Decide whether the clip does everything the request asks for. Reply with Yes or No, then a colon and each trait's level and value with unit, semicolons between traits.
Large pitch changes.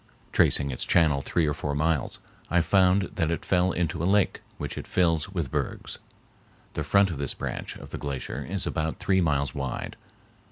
No: average, 4.3 semitones